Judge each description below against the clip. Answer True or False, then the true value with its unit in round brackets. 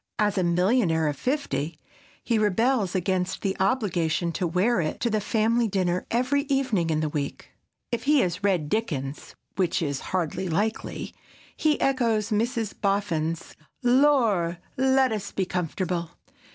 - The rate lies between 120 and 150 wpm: True (145 wpm)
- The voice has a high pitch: True (195 Hz)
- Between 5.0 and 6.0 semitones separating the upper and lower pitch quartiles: True (5.4 semitones)